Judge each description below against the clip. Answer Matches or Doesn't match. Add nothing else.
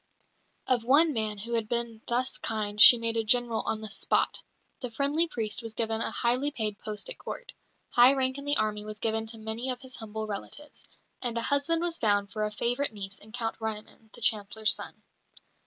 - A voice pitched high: Matches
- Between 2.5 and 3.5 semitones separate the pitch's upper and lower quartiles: Matches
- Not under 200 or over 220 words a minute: Matches